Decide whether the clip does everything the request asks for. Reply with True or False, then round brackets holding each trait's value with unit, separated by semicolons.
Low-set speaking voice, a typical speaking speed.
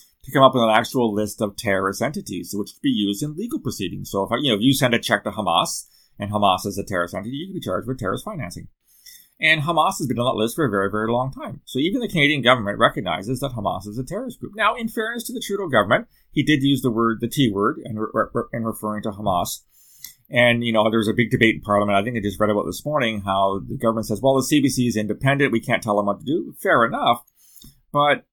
False (115 Hz; 265 wpm)